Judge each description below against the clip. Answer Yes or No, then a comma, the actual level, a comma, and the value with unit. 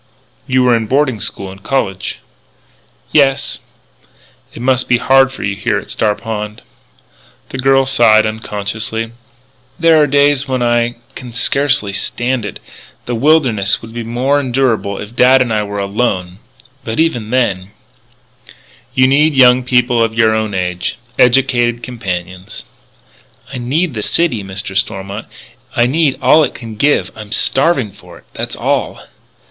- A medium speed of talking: Yes, average, 155 wpm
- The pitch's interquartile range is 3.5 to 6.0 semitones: Yes, average, 4.1 semitones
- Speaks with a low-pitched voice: Yes, low, 120 Hz